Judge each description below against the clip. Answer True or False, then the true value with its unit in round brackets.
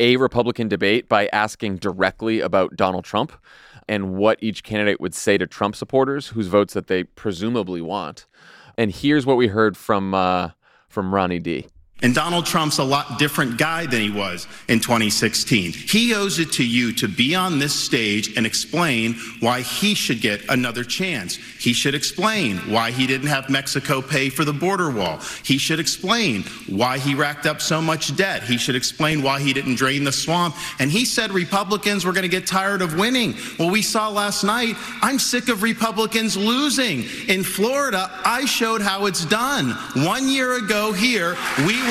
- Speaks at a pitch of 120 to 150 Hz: True (140 Hz)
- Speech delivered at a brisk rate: False (185 wpm)